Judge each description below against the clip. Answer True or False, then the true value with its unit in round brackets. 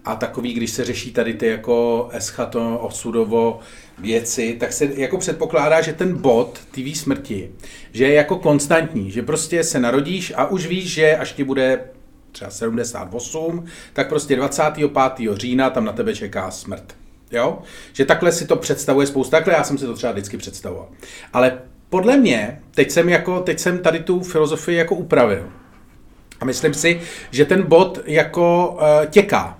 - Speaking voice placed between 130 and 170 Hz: True (140 Hz)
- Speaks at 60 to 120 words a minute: False (170 wpm)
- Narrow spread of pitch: False (5.6 semitones)